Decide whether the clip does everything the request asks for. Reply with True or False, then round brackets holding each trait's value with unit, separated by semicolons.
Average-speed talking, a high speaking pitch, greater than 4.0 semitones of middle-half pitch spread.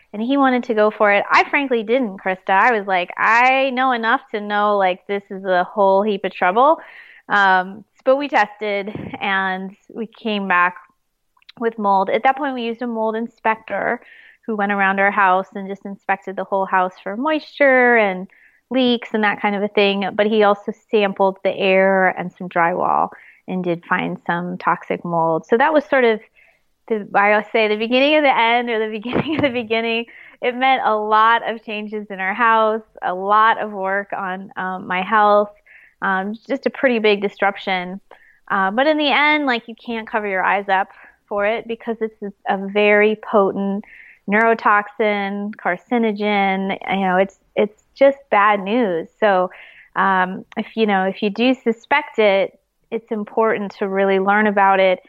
False (185 wpm; 210 Hz; 3.1 semitones)